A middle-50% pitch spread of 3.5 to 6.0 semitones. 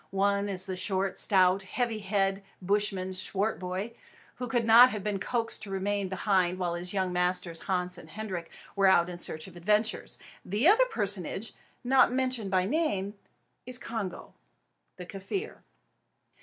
No: average, 2.9 semitones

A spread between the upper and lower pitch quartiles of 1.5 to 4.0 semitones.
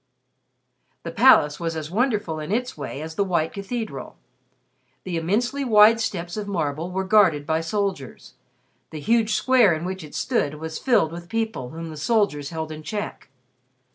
No: average, 5.3 semitones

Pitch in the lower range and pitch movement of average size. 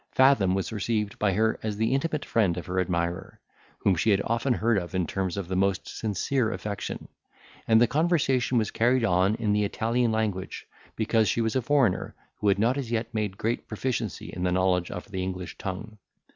Yes: low, 105 Hz; average, 3.8 semitones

